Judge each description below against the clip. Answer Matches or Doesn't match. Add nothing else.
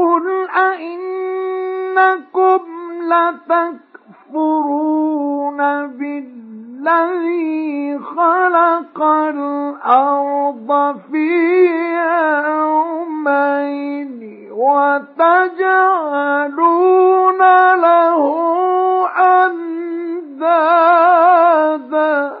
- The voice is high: Matches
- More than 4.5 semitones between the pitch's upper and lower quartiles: Doesn't match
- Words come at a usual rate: Doesn't match